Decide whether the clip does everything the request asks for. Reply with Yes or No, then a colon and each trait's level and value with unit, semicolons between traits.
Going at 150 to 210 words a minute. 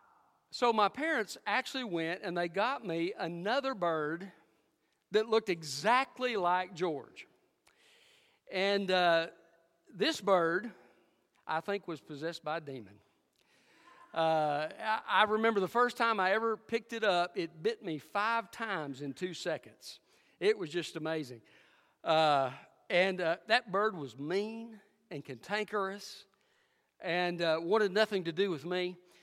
No: average, 140 wpm